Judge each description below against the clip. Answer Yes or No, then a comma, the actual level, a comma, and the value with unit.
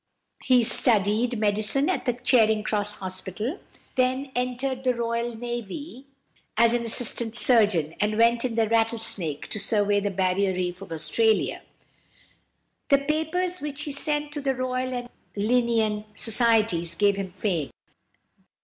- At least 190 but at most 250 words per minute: No, average, 140 wpm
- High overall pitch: Yes, high, 230 Hz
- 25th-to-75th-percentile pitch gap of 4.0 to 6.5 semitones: No, average, 3.6 semitones